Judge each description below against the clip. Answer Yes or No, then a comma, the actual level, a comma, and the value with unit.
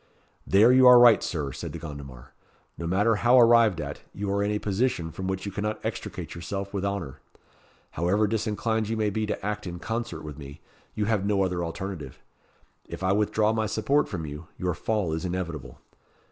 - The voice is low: Yes, low, 100 Hz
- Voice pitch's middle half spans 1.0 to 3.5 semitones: No, average, 4.2 semitones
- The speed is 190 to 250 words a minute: Yes, average, 195 wpm